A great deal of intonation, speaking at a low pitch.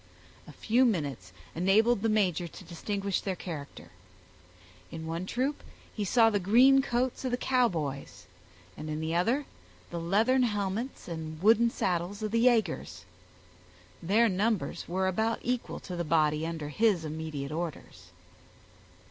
No: wide, 6.0 semitones; high, 190 Hz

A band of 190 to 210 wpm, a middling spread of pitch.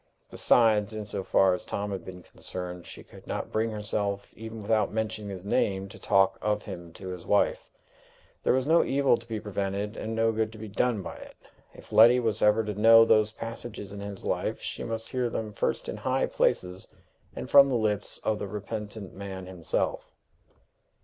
No: average, 195 wpm; narrow, 2.3 semitones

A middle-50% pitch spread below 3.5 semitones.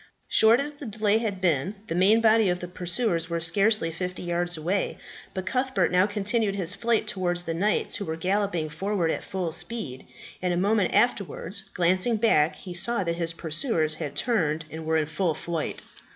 No: average, 4.0 semitones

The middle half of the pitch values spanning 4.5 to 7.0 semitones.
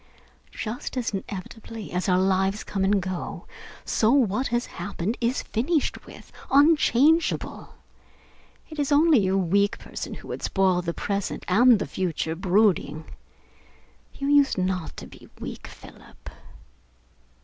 Yes: average, 5.2 semitones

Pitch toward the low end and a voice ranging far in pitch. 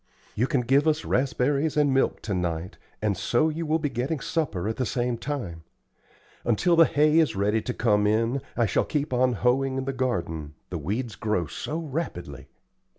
Yes: low, 125 Hz; wide, 5.7 semitones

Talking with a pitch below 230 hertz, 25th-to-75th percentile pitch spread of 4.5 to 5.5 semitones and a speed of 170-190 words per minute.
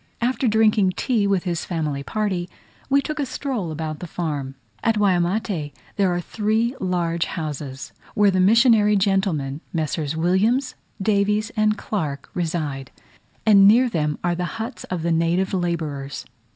No: medium, 185 Hz; average, 4.9 semitones; average, 150 wpm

